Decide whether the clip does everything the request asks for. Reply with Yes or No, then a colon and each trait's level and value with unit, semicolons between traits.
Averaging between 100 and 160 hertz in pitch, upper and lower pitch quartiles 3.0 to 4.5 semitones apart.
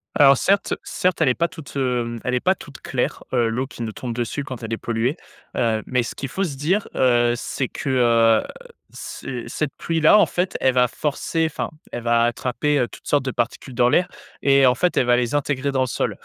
Yes: low, 130 Hz; average, 3.4 semitones